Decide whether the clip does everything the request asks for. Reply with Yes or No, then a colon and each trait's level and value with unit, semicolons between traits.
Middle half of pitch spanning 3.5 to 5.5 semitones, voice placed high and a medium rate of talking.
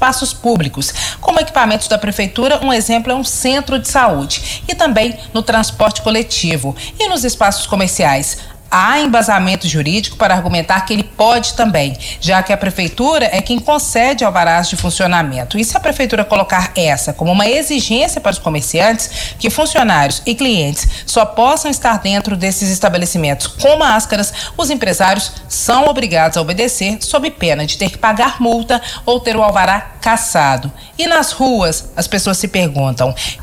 Yes: average, 5.2 semitones; high, 215 Hz; average, 160 wpm